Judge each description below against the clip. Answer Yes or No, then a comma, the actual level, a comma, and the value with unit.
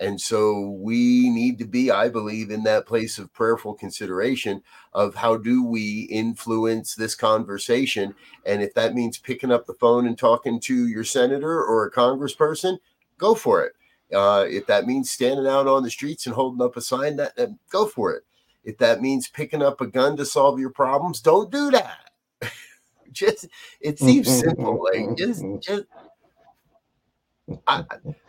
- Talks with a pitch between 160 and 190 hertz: No, low, 130 Hz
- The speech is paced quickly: No, average, 170 wpm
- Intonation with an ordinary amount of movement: No, wide, 6.1 semitones